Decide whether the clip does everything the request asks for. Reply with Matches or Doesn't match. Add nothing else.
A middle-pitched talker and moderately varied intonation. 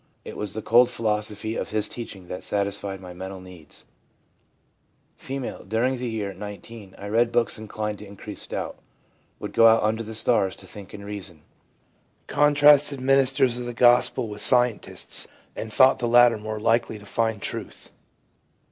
Doesn't match